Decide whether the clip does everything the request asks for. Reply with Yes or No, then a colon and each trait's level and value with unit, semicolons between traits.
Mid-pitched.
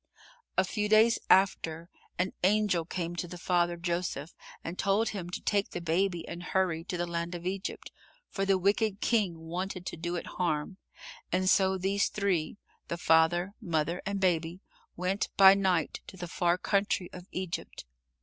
Yes: medium, 180 Hz